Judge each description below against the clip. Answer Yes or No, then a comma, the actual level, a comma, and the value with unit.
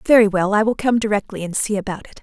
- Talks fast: Yes, fast, 270 wpm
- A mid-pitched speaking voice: No, high, 210 Hz